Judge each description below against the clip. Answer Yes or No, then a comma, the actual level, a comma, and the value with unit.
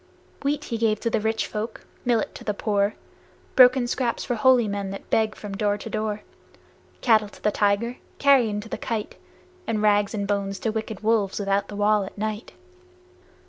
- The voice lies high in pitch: Yes, high, 215 Hz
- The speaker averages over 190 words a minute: No, average, 180 wpm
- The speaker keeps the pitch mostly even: Yes, narrow, 2.0 semitones